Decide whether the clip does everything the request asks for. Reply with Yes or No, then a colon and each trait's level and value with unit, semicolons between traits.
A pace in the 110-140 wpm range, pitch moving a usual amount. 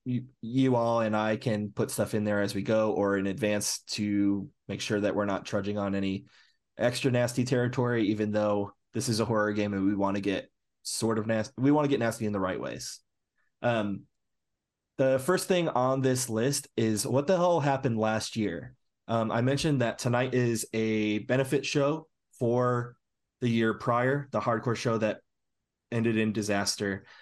No: average, 190 wpm; average, 3.2 semitones